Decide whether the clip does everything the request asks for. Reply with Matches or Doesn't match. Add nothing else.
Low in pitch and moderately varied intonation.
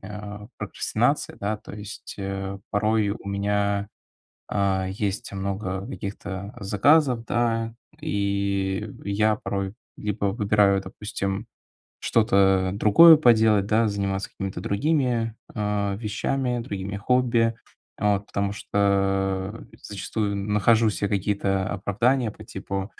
Doesn't match